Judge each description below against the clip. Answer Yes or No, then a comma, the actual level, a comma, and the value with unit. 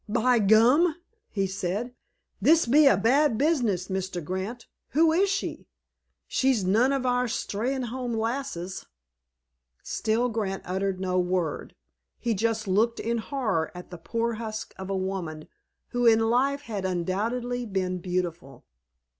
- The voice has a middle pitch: No, high, 220 Hz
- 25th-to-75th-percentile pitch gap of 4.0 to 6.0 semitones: Yes, average, 4.7 semitones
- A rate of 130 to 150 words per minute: Yes, average, 140 wpm